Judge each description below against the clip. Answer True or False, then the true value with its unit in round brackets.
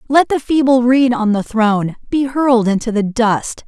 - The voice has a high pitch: True (240 Hz)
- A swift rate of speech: False (195 wpm)